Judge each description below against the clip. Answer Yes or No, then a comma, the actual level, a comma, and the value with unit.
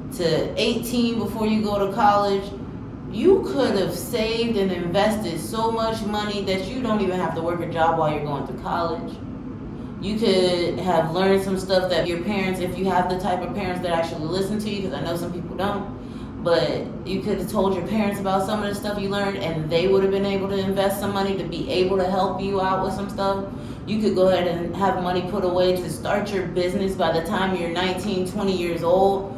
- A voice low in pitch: No, high, 190 Hz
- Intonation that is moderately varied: No, narrow, 2.1 semitones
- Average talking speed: No, fast, 230 wpm